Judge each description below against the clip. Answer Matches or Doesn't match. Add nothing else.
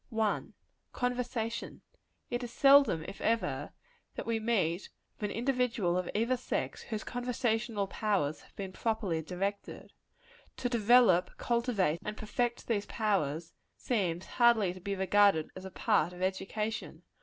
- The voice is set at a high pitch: Matches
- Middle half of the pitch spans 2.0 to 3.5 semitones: Doesn't match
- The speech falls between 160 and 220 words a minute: Doesn't match